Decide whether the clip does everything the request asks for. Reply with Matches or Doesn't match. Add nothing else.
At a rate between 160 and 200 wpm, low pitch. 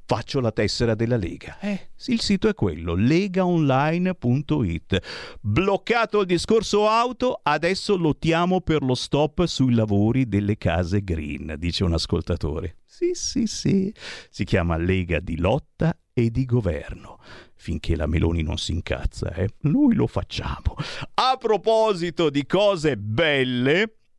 Doesn't match